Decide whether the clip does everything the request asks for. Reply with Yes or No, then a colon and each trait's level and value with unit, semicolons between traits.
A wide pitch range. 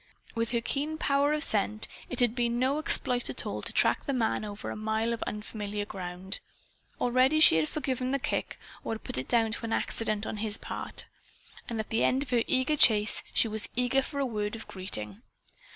No: average, 3.5 semitones